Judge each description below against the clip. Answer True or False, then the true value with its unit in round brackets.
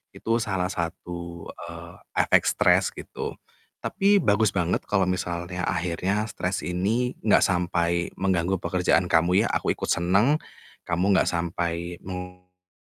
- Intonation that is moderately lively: False (2.0 semitones)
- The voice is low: True (90 Hz)